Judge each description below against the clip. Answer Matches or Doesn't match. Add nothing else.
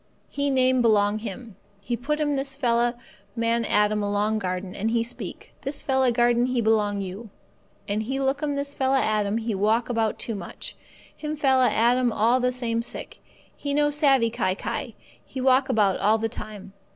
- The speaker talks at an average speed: Matches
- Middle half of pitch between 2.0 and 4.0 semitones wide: Matches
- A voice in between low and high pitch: Doesn't match